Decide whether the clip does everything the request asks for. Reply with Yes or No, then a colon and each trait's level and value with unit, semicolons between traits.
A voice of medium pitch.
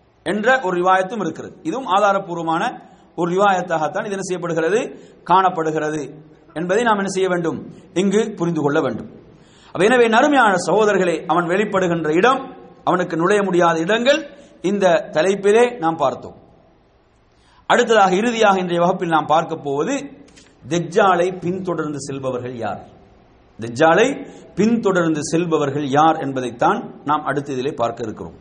Yes: medium, 175 Hz